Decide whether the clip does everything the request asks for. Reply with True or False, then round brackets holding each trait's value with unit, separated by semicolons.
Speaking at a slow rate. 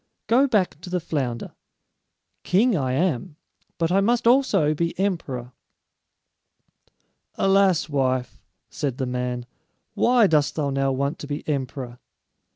True (130 wpm)